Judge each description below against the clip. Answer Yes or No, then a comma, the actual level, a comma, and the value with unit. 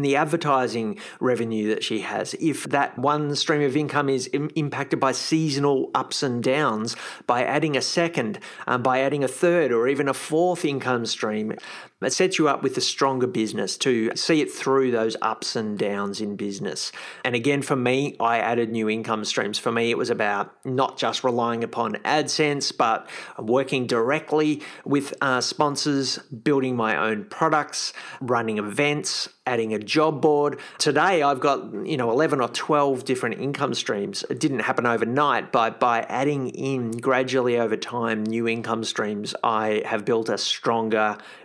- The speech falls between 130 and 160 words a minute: No, average, 170 wpm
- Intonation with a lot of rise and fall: No, average, 4.0 semitones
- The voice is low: Yes, low, 130 Hz